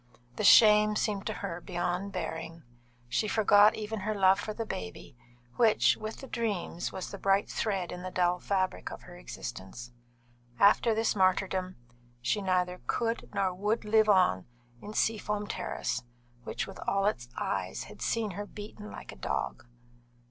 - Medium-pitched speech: No, high, 195 Hz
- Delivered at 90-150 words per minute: No, average, 165 wpm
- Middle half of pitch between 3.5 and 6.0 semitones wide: No, average, 3.0 semitones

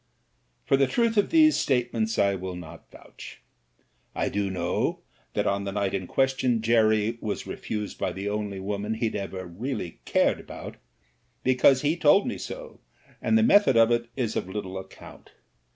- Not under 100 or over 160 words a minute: No, average, 175 wpm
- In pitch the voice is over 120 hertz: No, low, 110 Hz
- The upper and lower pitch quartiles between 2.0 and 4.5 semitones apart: No, average, 5.2 semitones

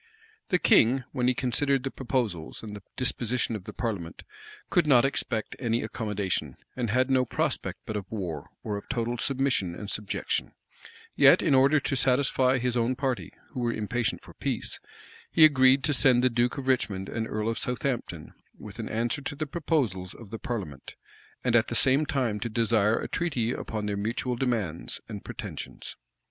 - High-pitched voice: No, low, 120 Hz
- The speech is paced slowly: No, average, 180 wpm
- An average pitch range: Yes, average, 3.6 semitones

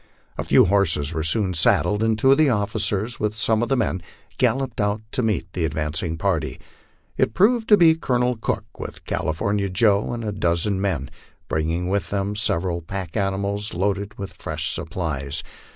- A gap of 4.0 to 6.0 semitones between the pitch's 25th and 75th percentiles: Yes, average, 4.6 semitones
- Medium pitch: No, low, 100 Hz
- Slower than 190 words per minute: Yes, average, 175 wpm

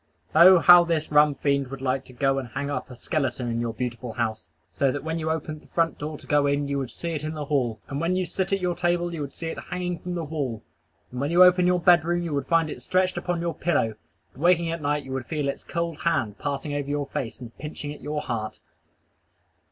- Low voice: No, medium, 150 Hz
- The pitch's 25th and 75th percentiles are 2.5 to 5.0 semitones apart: Yes, average, 3.9 semitones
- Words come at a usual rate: No, fast, 260 wpm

